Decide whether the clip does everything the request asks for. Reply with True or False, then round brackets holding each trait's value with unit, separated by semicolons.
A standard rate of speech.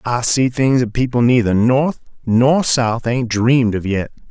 True (180 wpm)